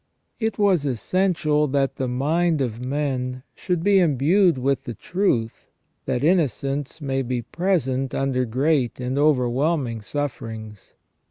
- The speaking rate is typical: No, slow, 125 wpm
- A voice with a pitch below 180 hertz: Yes, medium, 140 Hz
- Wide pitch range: No, average, 4.3 semitones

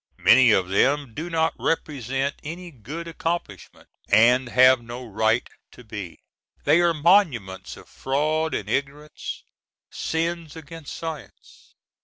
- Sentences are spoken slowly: Yes, slow, 120 wpm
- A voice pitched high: No, medium, 140 Hz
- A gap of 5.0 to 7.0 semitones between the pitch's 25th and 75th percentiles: Yes, average, 5.3 semitones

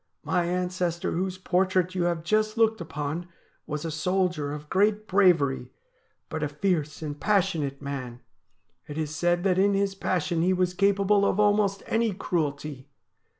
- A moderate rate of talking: Yes, average, 155 wpm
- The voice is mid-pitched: Yes, medium, 180 Hz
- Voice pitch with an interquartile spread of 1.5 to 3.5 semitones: No, average, 4.3 semitones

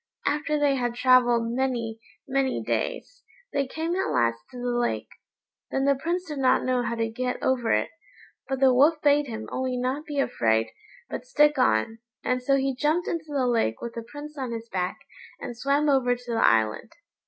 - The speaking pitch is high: Yes, very high, 255 Hz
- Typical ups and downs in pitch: Yes, average, 3.5 semitones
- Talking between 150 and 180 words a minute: No, average, 195 wpm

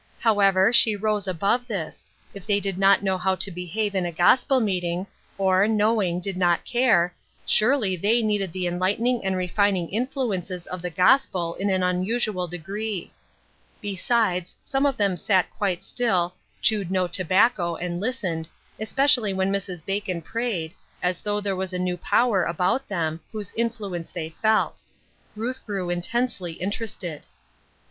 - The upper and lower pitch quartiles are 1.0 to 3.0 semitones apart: No, average, 3.4 semitones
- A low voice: No, high, 195 Hz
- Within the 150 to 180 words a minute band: Yes, average, 155 wpm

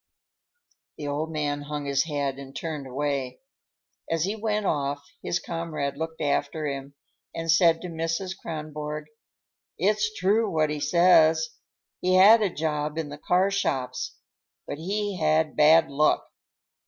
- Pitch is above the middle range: No, medium, 155 Hz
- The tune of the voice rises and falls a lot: No, average, 3.2 semitones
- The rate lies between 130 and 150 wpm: Yes, average, 145 wpm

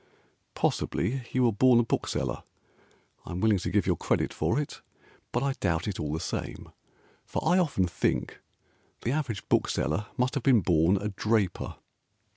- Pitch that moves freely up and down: Yes, wide, 6.1 semitones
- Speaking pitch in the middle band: No, low, 105 Hz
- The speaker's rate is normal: Yes, average, 170 wpm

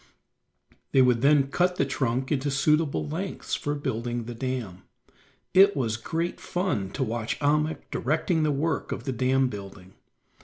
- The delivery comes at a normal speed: Yes, average, 155 wpm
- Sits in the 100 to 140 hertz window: Yes, low, 135 Hz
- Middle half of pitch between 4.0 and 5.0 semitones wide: Yes, average, 4.3 semitones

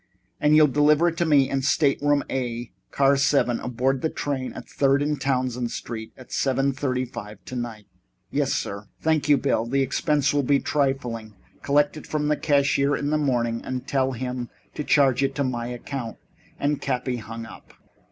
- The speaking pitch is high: No, low, 135 Hz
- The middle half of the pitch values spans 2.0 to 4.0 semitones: Yes, average, 2.8 semitones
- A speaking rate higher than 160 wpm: Yes, average, 180 wpm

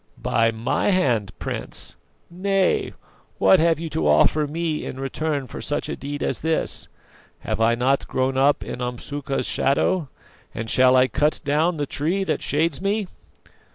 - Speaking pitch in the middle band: Yes, medium, 145 Hz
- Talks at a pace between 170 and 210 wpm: No, average, 160 wpm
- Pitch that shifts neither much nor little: Yes, average, 4.2 semitones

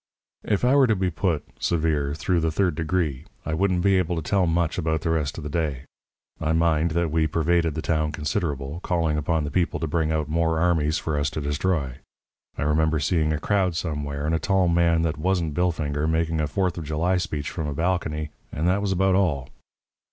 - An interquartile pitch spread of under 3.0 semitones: Yes, narrow, 2.6 semitones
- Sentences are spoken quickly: Yes, fast, 215 wpm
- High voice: No, very low, 80 Hz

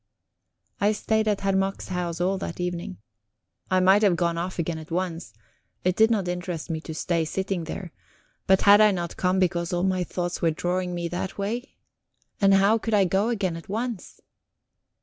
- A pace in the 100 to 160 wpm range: No, average, 190 wpm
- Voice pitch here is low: No, medium, 185 Hz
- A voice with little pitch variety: Yes, narrow, 2.3 semitones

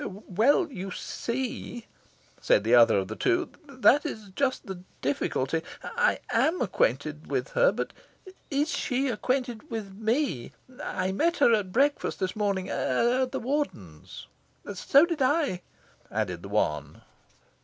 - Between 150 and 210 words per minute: No, average, 140 wpm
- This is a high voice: Yes, high, 230 Hz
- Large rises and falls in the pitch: Yes, wide, 7.5 semitones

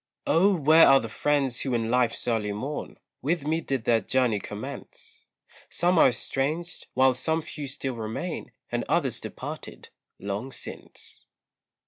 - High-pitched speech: No, low, 135 Hz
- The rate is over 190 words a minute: No, average, 145 wpm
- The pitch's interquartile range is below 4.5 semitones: No, average, 5.2 semitones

